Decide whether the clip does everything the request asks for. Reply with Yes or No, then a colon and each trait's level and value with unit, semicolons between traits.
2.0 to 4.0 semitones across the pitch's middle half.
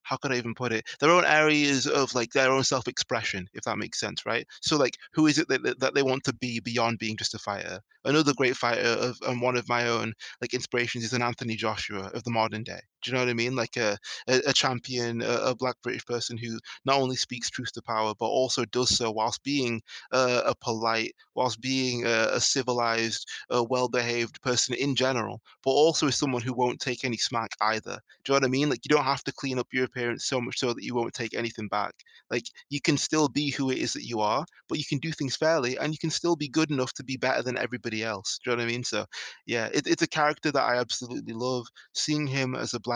Yes: narrow, 2.5 semitones